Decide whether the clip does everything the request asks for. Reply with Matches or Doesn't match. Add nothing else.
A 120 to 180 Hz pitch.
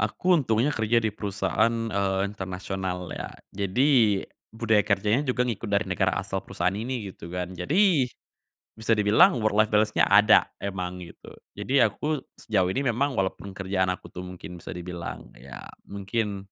Doesn't match